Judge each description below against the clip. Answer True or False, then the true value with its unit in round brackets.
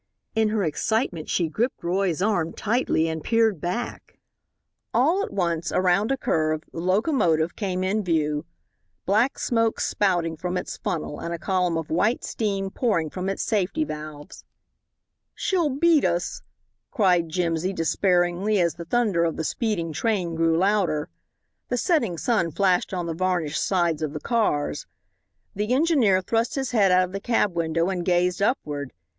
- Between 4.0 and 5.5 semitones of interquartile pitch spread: True (4.6 semitones)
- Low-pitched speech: False (185 Hz)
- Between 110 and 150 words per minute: False (160 wpm)